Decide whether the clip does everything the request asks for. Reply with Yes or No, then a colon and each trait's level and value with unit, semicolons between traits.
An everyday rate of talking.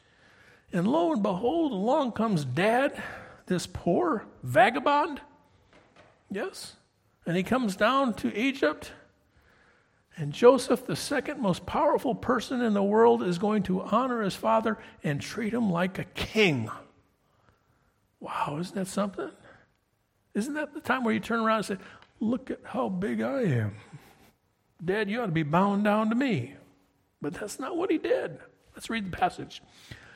Yes: average, 155 wpm